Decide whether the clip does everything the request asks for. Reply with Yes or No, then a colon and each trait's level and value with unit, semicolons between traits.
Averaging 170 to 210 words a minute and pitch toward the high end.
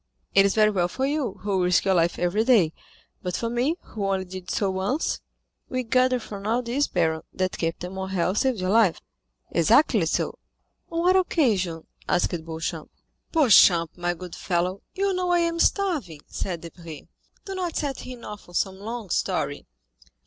Yes: average, 175 wpm; high, 200 Hz